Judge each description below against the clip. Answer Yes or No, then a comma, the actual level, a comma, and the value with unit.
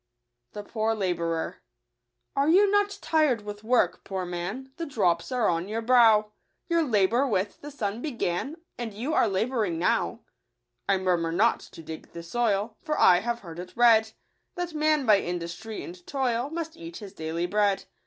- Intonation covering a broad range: Yes, wide, 6.6 semitones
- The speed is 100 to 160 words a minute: No, average, 185 wpm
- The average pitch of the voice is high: Yes, high, 215 Hz